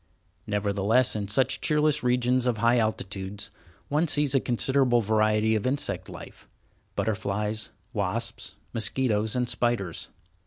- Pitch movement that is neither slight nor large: Yes, average, 3.4 semitones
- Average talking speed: No, slow, 115 wpm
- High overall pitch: No, low, 110 Hz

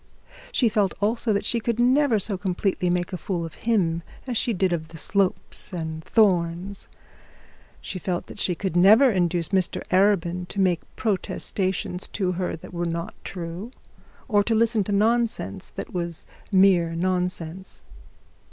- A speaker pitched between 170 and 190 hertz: Yes, medium, 185 Hz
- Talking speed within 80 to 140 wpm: No, average, 160 wpm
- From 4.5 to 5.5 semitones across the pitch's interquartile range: No, average, 3.3 semitones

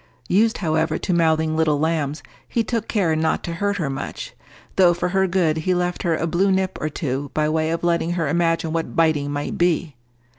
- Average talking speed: No, fast, 210 wpm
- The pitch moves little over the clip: Yes, narrow, 2.3 semitones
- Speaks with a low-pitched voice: No, medium, 165 Hz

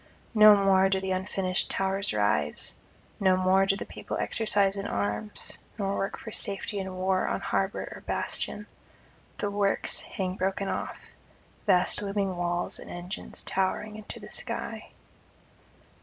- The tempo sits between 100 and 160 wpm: Yes, average, 145 wpm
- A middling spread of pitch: No, narrow, 1.4 semitones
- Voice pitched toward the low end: No, high, 195 Hz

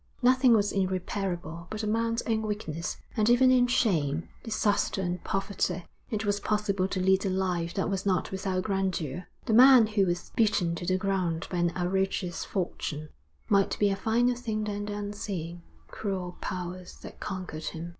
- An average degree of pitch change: Yes, average, 3.1 semitones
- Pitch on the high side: Yes, high, 195 Hz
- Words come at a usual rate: Yes, average, 175 wpm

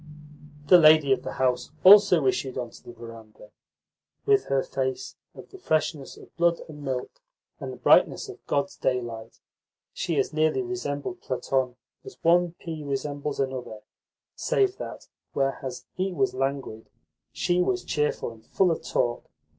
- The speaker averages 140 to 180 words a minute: Yes, average, 155 wpm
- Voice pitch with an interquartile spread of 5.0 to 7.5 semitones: Yes, average, 5.3 semitones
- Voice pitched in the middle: Yes, medium, 145 Hz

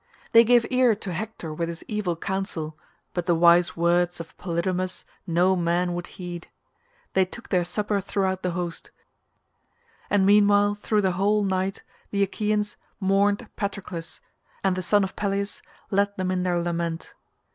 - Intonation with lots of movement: No, narrow, 2.6 semitones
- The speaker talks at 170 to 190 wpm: No, average, 155 wpm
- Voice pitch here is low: No, high, 190 Hz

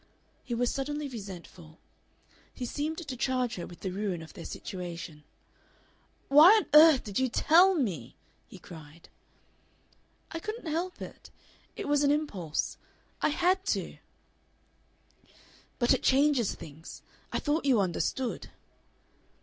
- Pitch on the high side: Yes, very high, 255 Hz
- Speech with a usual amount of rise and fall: No, wide, 8.7 semitones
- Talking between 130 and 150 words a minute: Yes, slow, 135 wpm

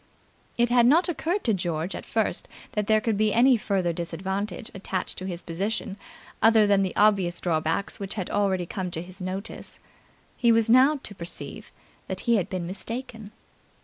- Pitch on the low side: No, high, 200 Hz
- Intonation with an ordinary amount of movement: Yes, average, 3.6 semitones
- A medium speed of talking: Yes, average, 180 wpm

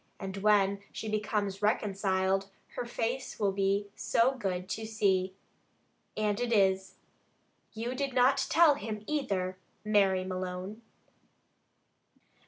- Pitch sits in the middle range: No, high, 205 Hz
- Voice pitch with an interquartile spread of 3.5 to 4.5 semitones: No, average, 2.8 semitones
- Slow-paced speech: Yes, slow, 115 wpm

